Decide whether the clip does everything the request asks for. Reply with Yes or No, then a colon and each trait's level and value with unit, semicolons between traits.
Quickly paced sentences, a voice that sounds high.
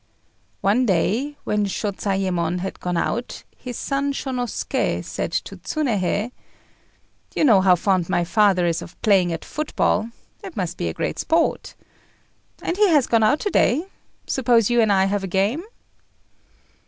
No: average, 155 wpm; high, 210 Hz